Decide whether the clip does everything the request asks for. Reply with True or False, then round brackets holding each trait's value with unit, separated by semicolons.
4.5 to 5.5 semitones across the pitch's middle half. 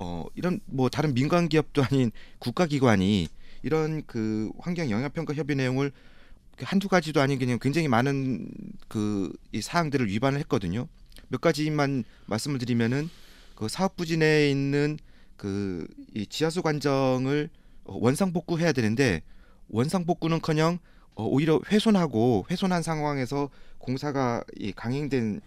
True (5.1 semitones)